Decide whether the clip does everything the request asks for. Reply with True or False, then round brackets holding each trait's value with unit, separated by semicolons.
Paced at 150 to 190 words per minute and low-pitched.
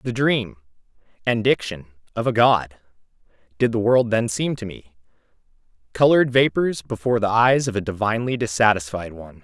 False (140 wpm; 110 Hz)